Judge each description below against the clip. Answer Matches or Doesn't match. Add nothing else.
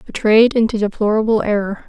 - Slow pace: Matches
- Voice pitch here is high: Matches